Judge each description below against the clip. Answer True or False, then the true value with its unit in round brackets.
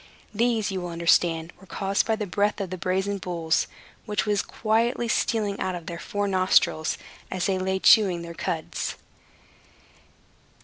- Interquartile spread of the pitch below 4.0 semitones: True (3.0 semitones)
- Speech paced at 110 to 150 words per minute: False (160 wpm)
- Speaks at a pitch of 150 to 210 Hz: True (190 Hz)